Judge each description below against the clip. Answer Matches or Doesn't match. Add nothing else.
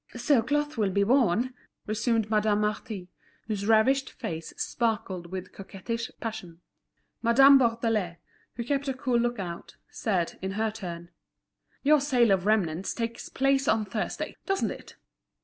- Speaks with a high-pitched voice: Matches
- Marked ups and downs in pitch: Doesn't match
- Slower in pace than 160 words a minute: Matches